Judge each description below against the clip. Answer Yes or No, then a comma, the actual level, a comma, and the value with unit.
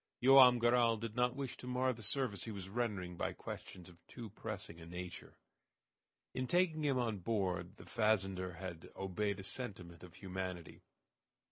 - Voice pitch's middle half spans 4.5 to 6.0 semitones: Yes, average, 5.1 semitones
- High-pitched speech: No, low, 105 Hz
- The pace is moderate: Yes, average, 165 wpm